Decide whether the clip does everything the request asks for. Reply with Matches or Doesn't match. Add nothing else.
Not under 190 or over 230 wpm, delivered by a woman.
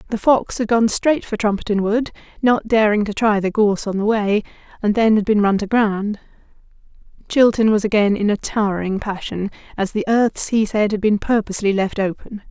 Matches